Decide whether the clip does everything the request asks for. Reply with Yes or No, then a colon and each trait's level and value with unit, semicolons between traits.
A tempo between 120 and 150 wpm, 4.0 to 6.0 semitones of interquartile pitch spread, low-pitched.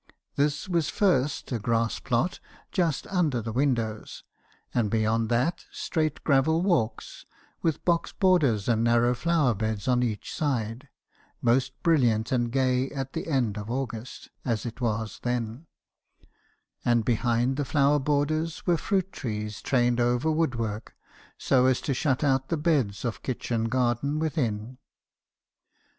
Yes: average, 145 wpm; average, 4.3 semitones; low, 125 Hz